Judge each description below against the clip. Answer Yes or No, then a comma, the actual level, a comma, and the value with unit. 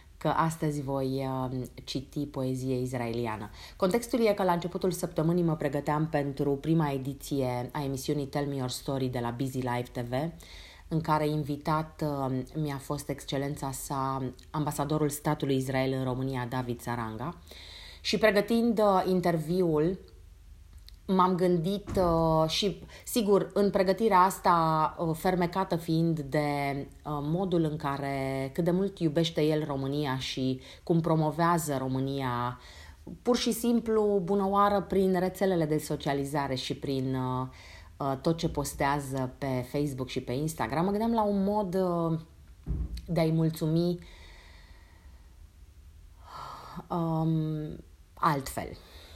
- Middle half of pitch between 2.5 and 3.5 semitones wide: No, average, 4.8 semitones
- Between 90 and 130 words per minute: Yes, average, 120 wpm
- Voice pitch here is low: No, medium, 150 Hz